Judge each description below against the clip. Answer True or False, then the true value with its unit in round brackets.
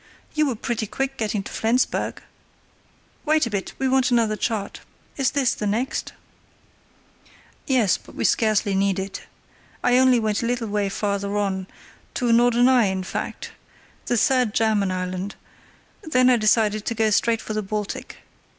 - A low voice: False (220 Hz)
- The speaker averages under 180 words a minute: True (150 wpm)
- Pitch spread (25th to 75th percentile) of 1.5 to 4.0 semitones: True (3.4 semitones)